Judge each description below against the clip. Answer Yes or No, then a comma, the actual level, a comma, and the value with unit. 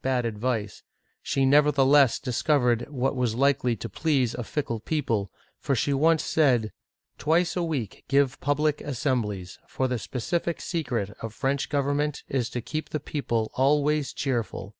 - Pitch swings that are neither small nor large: Yes, average, 3.9 semitones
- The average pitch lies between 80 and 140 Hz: Yes, low, 135 Hz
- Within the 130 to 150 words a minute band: No, average, 160 wpm